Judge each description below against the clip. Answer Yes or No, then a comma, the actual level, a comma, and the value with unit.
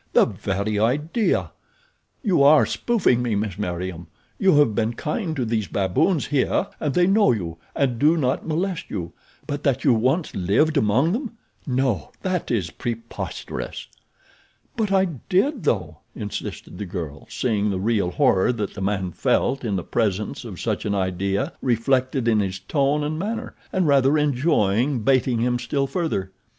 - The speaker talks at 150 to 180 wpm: Yes, average, 160 wpm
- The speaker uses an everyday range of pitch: No, wide, 7.0 semitones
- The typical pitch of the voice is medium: No, low, 125 Hz